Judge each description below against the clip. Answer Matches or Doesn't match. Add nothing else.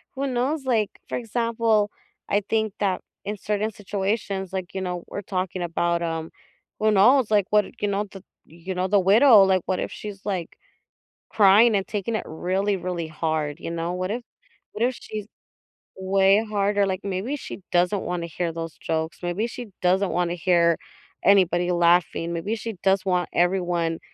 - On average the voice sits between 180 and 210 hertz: Matches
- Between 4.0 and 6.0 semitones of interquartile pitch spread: Doesn't match